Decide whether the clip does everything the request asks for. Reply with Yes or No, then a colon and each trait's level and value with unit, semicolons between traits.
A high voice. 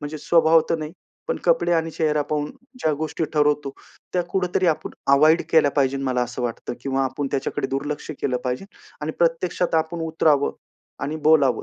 No: medium, 150 Hz